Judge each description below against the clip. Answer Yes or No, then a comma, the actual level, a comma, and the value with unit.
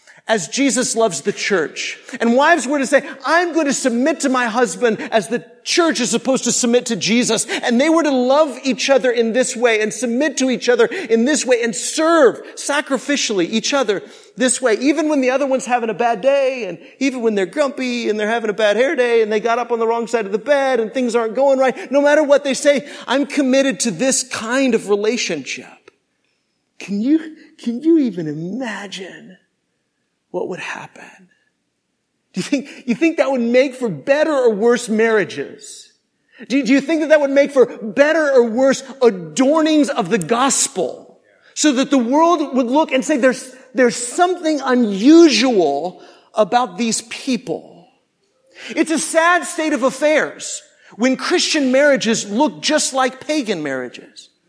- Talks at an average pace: Yes, average, 185 wpm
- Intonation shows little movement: No, average, 3.8 semitones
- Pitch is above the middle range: Yes, very high, 260 Hz